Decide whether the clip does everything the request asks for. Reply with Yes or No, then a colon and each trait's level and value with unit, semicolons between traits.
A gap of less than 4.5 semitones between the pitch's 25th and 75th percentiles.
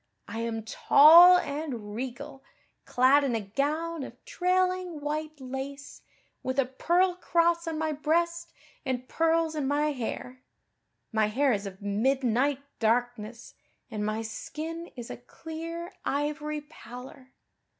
No: average, 4.8 semitones